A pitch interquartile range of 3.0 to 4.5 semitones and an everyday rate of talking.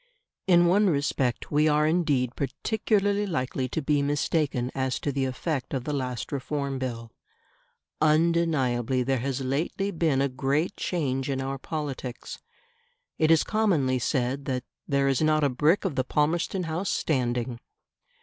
Yes: average, 3.6 semitones; average, 150 wpm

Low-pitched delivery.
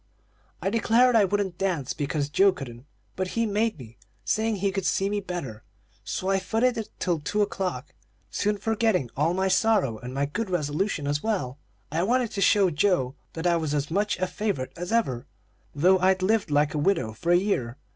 No: medium, 185 Hz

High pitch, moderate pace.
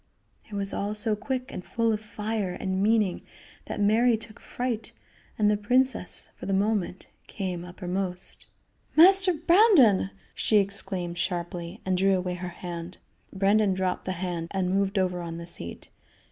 Yes: high, 195 Hz; average, 160 wpm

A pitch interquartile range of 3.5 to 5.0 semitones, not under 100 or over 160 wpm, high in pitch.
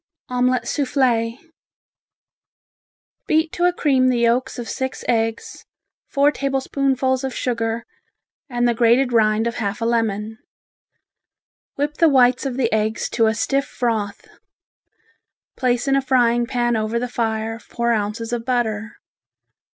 No: narrow, 2.5 semitones; slow, 135 wpm; high, 240 Hz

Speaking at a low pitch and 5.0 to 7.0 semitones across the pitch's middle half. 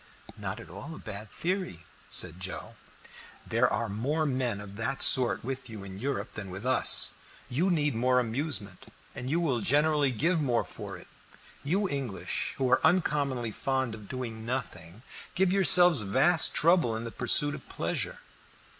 Yes: low, 130 Hz; average, 5.3 semitones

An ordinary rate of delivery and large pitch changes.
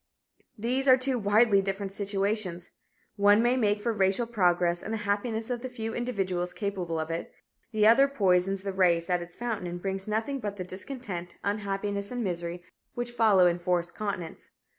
No: average, 175 wpm; average, 3.8 semitones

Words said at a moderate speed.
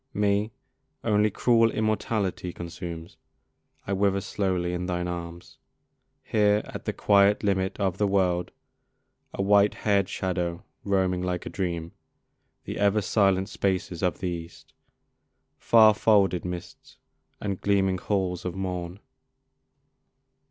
No: slow, 125 wpm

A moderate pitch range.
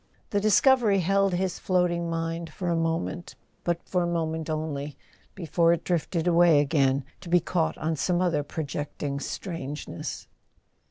No: narrow, 2.3 semitones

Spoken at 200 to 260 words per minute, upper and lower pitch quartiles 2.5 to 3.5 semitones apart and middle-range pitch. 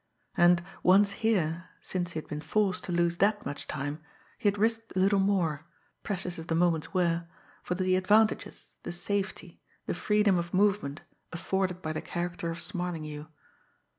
No: average, 165 wpm; average, 3.0 semitones; medium, 180 Hz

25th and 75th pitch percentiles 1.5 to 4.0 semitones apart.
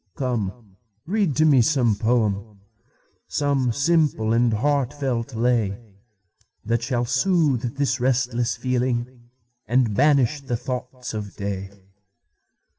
Yes: average, 3.1 semitones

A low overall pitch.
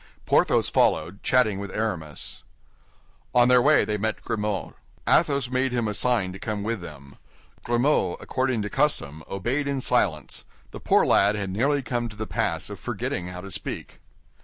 Yes: low, 110 Hz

